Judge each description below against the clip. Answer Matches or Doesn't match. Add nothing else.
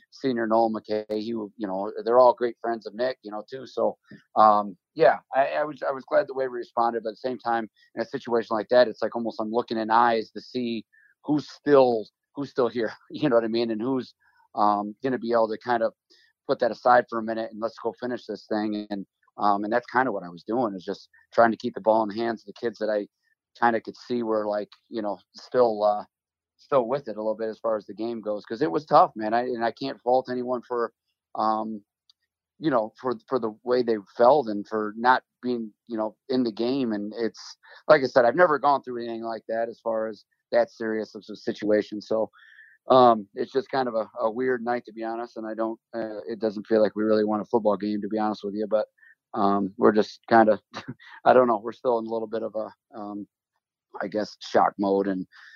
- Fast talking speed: Matches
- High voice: Doesn't match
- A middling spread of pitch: Doesn't match